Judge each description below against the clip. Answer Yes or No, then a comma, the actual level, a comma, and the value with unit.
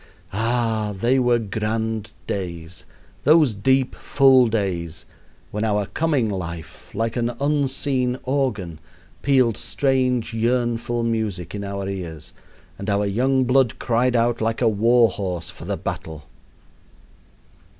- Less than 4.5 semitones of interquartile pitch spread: Yes, average, 4.1 semitones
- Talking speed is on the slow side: Yes, slow, 125 wpm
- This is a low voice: Yes, low, 115 Hz